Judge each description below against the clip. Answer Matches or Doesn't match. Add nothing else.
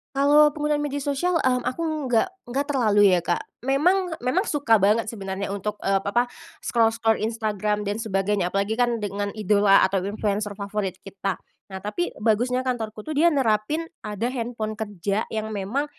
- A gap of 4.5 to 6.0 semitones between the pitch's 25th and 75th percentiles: Matches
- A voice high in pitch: Matches